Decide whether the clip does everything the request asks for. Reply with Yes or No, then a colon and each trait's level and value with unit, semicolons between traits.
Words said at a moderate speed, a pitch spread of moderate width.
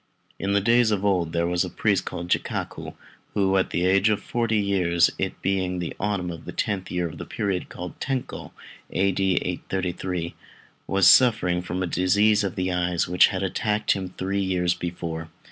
No: average, 180 wpm; narrow, 2.1 semitones